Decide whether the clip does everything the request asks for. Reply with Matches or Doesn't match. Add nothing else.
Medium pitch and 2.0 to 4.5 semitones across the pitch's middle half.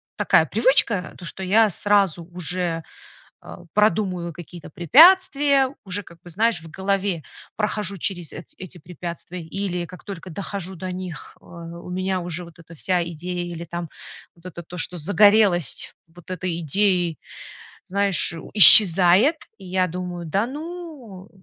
Matches